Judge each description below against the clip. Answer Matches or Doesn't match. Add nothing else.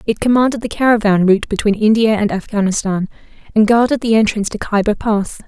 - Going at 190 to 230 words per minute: Doesn't match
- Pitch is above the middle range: Matches